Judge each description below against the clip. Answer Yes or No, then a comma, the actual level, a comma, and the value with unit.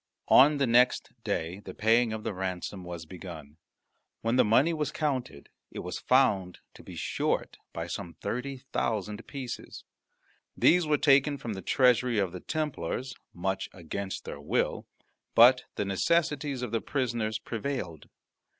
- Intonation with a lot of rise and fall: Yes, wide, 6.0 semitones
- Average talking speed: Yes, average, 150 wpm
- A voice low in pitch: Yes, low, 115 Hz